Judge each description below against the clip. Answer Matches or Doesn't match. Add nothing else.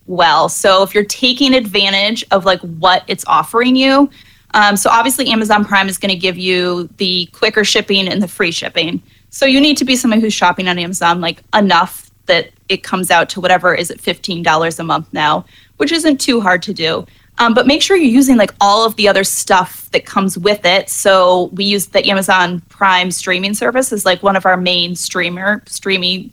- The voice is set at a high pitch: Matches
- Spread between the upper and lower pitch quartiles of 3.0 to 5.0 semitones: Matches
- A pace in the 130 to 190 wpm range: Doesn't match